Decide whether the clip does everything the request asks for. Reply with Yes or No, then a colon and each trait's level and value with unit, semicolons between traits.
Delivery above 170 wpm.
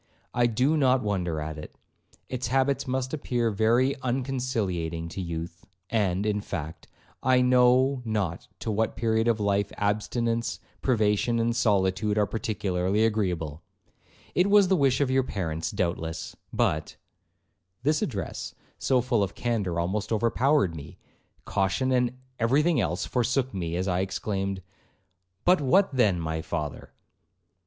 No: average, 140 wpm